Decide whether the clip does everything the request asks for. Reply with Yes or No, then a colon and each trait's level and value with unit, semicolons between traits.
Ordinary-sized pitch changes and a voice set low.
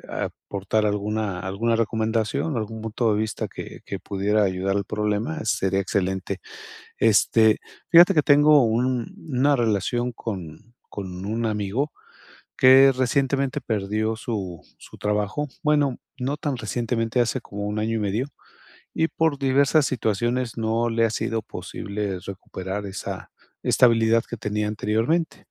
Yes: average, 3.6 semitones; low, 110 Hz